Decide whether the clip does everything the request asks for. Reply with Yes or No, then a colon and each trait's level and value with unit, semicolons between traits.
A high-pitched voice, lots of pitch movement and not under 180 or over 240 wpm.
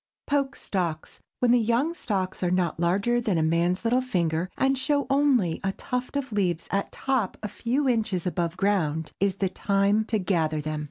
Yes: high, 200 Hz; wide, 5.9 semitones; average, 185 wpm